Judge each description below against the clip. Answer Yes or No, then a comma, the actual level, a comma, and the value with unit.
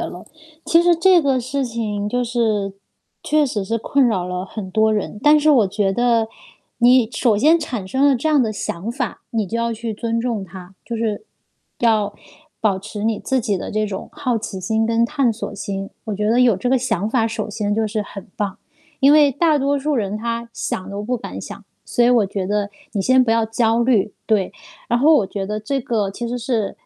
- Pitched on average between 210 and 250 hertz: Yes, high, 225 Hz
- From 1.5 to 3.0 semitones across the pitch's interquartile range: No, average, 3.4 semitones